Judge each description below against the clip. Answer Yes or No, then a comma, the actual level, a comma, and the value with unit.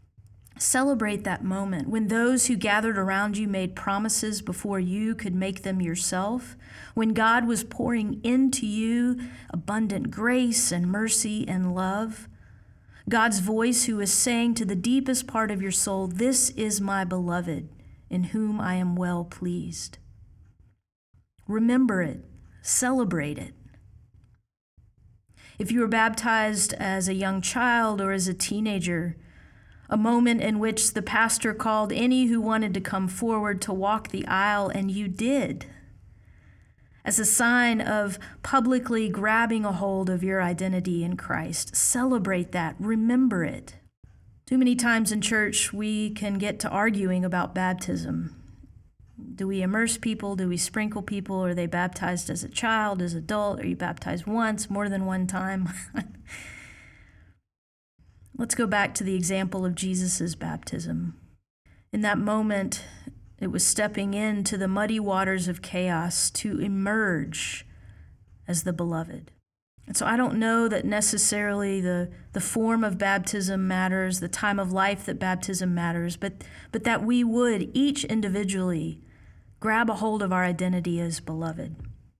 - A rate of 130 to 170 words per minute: Yes, average, 145 wpm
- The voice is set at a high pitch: Yes, high, 195 Hz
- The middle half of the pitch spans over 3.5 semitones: Yes, average, 4.0 semitones